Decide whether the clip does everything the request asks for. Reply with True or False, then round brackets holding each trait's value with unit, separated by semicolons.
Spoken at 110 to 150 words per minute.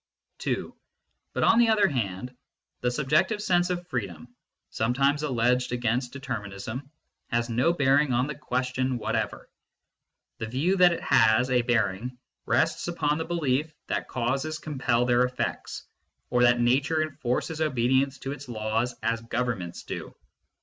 True (145 wpm)